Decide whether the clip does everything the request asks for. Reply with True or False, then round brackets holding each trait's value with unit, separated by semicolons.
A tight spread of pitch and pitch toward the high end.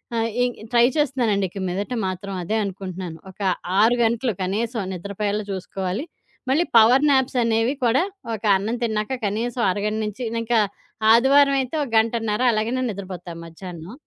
False (3.7 semitones; 220 Hz)